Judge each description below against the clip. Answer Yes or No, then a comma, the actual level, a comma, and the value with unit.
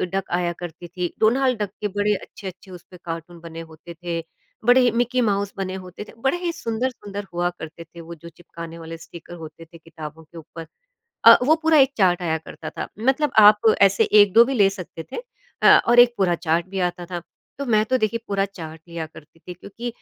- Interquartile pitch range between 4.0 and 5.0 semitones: Yes, average, 4.7 semitones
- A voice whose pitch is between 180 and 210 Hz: Yes, medium, 185 Hz